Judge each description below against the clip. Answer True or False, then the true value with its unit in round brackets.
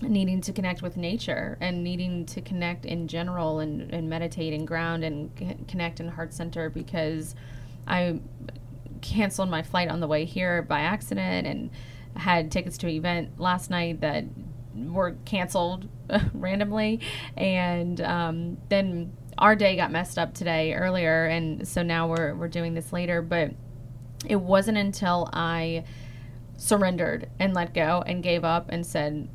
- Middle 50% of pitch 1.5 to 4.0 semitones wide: True (2.7 semitones)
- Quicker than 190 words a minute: False (155 wpm)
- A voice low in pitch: False (170 Hz)